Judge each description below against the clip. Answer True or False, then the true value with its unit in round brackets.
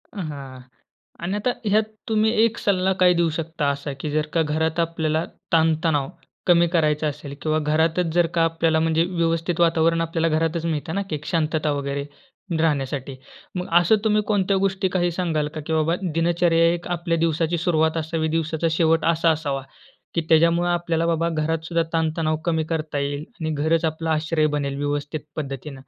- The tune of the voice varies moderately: False (1.6 semitones)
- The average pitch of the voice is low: False (160 Hz)